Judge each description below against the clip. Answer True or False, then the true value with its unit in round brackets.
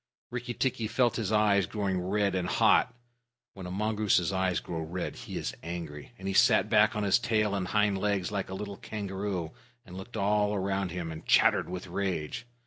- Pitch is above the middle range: False (100 Hz)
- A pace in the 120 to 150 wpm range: False (195 wpm)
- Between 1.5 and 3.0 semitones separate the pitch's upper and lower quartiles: True (2.5 semitones)